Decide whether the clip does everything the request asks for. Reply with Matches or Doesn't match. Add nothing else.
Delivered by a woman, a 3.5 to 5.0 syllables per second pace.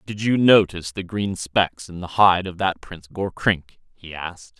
Doesn't match